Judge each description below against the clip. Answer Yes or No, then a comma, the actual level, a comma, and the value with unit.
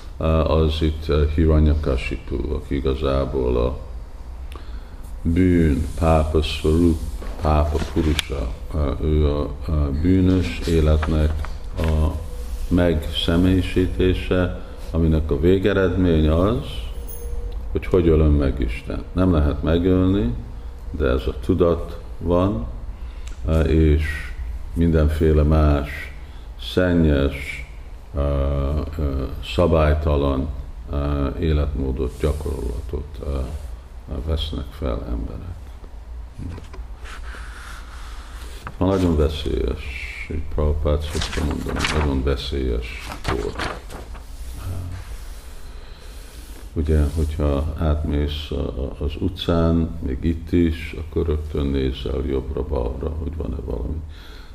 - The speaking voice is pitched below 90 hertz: Yes, very low, 75 Hz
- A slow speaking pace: Yes, slow, 85 wpm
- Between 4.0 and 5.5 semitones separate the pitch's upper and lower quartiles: No, average, 3.0 semitones